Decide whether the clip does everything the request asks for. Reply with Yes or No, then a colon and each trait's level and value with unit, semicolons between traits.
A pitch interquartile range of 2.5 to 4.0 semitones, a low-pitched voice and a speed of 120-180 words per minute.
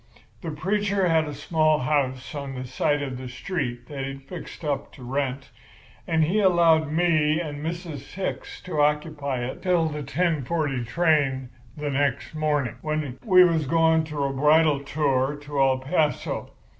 No: average, 3.0 semitones; medium, 150 Hz; average, 170 wpm